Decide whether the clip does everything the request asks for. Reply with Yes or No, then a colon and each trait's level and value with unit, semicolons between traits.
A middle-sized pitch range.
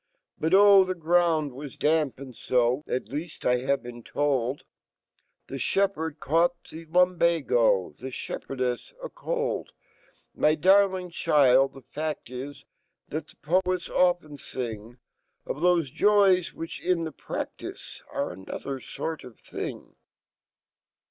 Yes: average, 5.0 semitones